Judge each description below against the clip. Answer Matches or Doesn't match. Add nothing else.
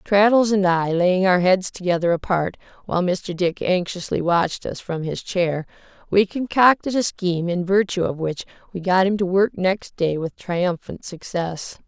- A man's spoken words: Doesn't match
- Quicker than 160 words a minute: Matches